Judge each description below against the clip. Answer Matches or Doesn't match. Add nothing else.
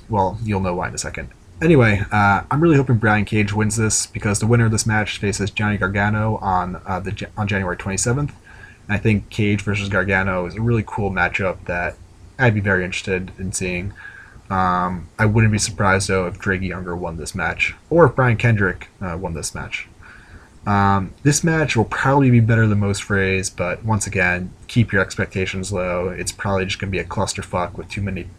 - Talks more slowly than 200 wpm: Doesn't match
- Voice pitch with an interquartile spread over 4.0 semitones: Doesn't match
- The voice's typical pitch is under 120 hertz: Matches